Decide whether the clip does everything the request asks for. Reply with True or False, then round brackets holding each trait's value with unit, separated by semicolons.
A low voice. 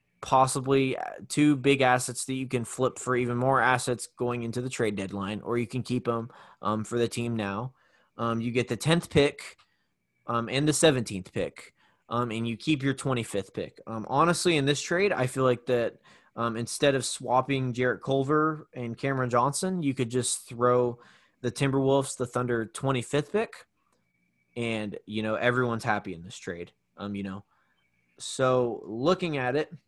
True (125 Hz)